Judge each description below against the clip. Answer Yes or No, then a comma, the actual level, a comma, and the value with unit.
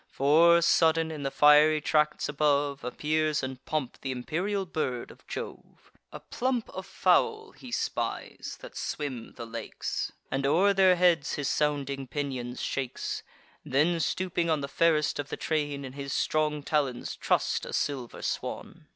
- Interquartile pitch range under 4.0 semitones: Yes, average, 3.3 semitones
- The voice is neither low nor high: Yes, medium, 150 Hz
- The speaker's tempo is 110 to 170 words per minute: Yes, average, 155 wpm